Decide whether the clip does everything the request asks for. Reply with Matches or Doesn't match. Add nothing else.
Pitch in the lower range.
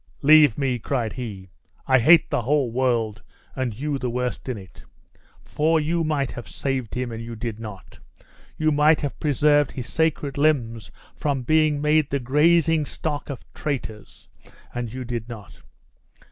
Matches